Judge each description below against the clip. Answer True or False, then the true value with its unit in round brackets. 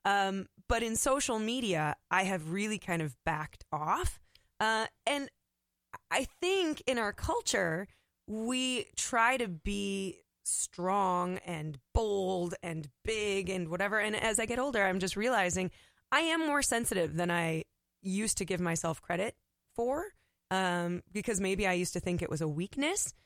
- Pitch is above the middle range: True (195 Hz)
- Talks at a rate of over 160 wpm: False (155 wpm)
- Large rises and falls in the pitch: False (4.5 semitones)